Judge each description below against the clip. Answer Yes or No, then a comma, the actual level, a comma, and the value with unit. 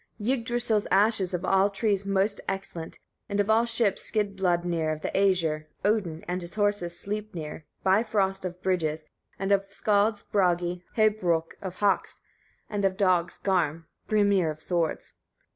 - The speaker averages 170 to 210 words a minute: No, average, 150 wpm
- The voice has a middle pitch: No, high, 195 Hz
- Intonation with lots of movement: No, average, 2.9 semitones